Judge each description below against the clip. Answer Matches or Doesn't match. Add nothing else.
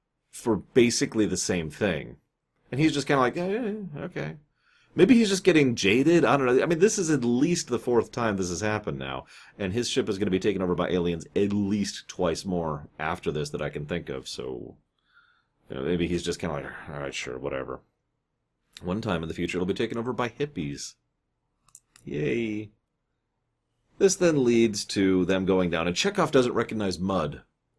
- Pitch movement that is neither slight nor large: Doesn't match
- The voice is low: Matches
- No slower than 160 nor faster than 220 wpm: Matches